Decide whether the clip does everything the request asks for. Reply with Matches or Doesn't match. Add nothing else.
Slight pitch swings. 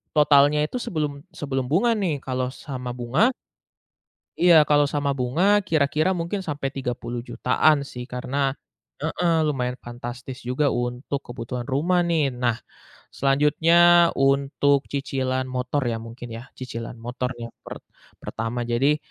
Doesn't match